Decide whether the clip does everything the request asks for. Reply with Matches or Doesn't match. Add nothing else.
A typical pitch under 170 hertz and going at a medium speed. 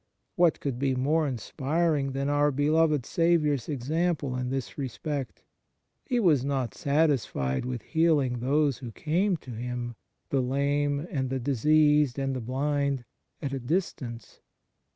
Matches